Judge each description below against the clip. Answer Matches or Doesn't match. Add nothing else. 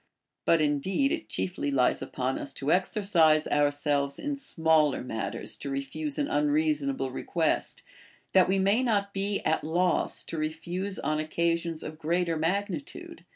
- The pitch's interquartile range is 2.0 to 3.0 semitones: Doesn't match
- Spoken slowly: Doesn't match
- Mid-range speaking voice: Matches